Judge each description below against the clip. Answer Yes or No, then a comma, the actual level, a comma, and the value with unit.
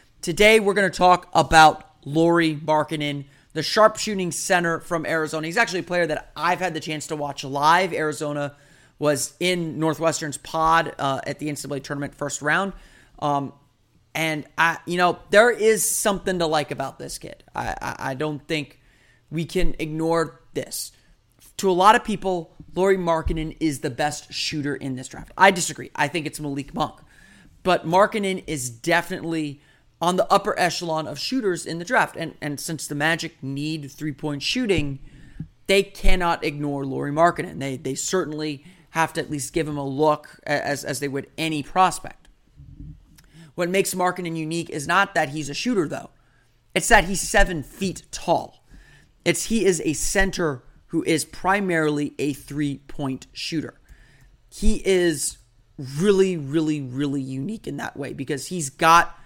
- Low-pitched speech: No, medium, 155 Hz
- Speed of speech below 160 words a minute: No, average, 165 wpm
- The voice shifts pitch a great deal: No, average, 3.5 semitones